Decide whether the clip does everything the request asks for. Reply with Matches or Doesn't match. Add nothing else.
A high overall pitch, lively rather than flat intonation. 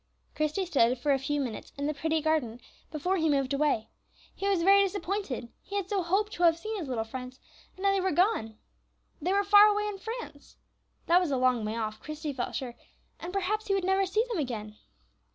Matches